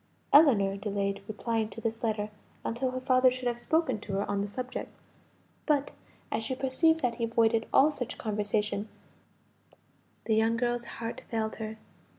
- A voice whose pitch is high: Yes, high, 230 Hz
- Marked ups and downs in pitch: No, average, 3.0 semitones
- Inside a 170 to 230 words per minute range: No, average, 160 wpm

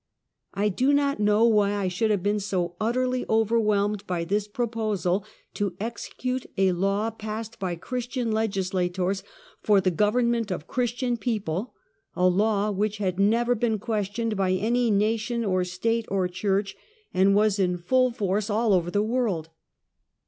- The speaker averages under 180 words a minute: Yes, average, 160 wpm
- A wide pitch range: No, average, 3.2 semitones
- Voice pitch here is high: Yes, high, 210 Hz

